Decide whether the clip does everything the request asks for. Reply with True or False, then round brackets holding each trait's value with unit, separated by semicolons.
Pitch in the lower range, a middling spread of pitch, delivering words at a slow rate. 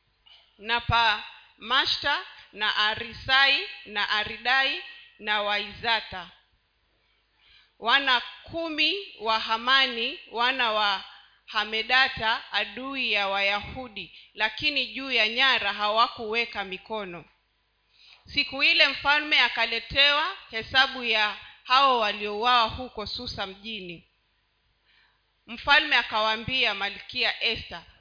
False (225 Hz; 4.3 semitones; 85 wpm)